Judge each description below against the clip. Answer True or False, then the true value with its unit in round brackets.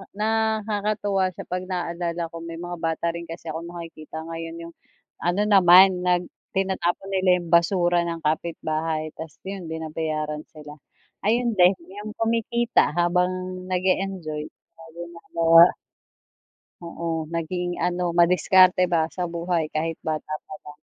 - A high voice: False (175 Hz)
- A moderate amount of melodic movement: False (2.3 semitones)